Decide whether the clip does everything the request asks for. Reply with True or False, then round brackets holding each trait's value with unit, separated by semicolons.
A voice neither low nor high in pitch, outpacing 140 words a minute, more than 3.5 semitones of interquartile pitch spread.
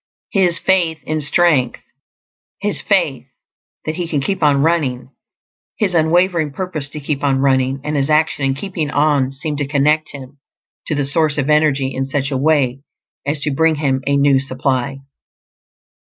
False (145 Hz; 165 wpm; 2.6 semitones)